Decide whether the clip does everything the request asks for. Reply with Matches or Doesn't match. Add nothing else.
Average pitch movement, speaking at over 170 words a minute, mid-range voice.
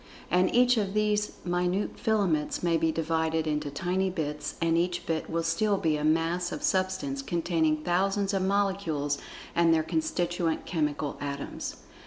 Doesn't match